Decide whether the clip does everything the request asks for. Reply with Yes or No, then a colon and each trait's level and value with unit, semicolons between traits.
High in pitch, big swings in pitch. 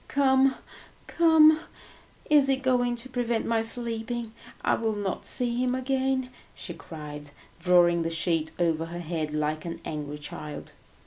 Yes: high, 225 Hz; wide, 7.9 semitones